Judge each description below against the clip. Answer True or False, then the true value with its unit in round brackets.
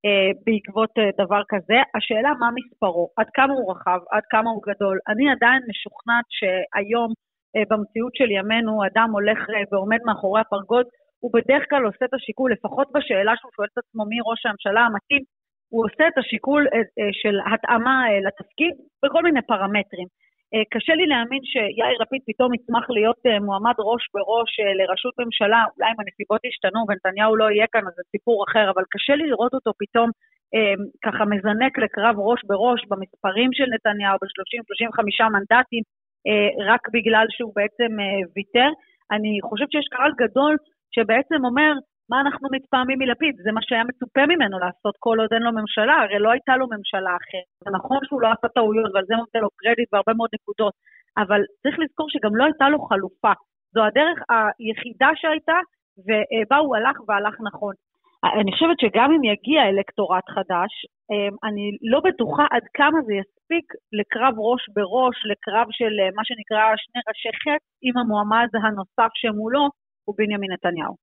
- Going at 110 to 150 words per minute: False (160 wpm)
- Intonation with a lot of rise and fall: False (3.6 semitones)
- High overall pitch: True (225 Hz)